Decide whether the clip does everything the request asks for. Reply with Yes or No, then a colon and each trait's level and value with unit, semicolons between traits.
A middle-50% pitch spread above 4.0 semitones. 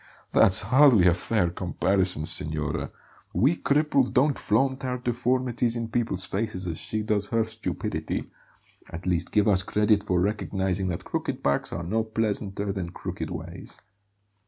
Yes: average, 4.4 semitones